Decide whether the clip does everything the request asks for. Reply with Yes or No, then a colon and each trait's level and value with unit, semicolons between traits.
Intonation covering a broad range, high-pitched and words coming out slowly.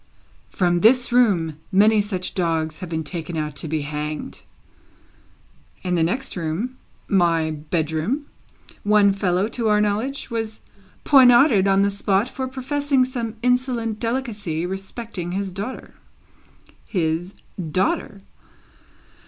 Yes: wide, 5.9 semitones; high, 200 Hz; slow, 120 wpm